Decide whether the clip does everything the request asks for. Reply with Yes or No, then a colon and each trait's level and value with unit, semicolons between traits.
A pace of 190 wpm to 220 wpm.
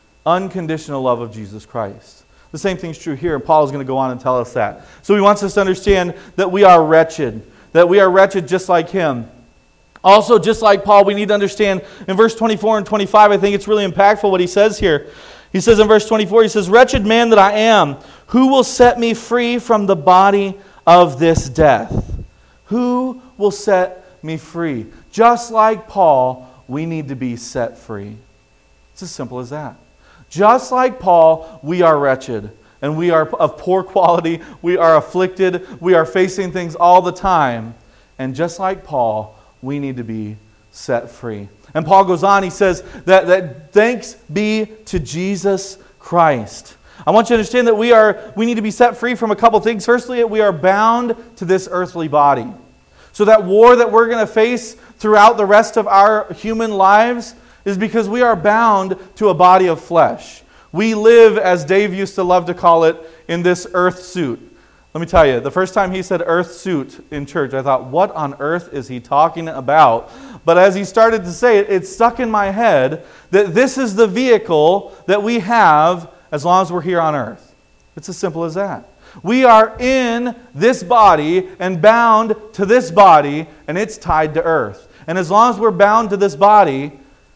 Yes: average, 200 wpm